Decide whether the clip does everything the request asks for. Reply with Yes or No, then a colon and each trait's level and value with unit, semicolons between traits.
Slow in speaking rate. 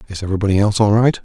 No: fast, 240 wpm